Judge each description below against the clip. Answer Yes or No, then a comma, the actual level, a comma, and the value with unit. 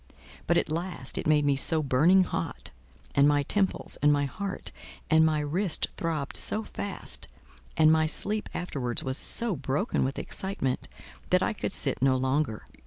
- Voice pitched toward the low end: No, medium, 155 Hz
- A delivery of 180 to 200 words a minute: No, average, 170 wpm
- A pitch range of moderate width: Yes, average, 4.6 semitones